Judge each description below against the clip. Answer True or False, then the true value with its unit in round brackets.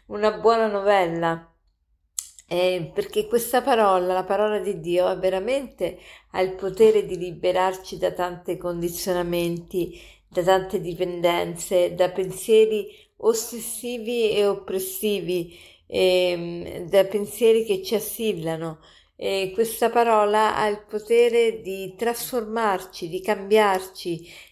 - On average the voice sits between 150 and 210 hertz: True (190 Hz)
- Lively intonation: False (3.3 semitones)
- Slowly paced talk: True (110 wpm)